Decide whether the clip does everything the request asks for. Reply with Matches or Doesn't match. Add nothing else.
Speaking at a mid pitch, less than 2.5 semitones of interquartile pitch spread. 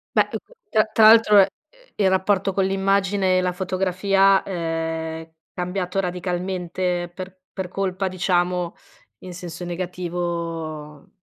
Matches